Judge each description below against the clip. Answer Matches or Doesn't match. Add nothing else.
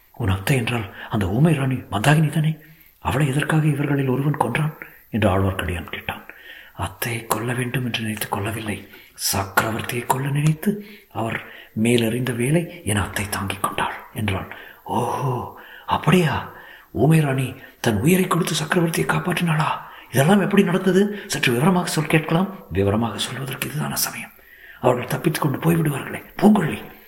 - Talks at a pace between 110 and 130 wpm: Matches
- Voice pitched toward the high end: Doesn't match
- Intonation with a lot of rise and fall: Matches